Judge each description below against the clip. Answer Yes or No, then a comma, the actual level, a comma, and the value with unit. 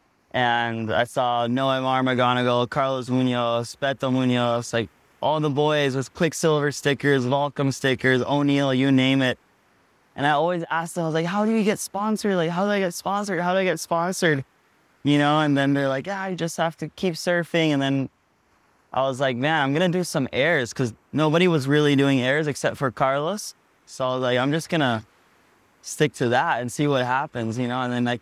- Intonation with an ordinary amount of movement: Yes, average, 4.2 semitones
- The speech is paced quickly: Yes, fast, 215 wpm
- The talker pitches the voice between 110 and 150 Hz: Yes, medium, 140 Hz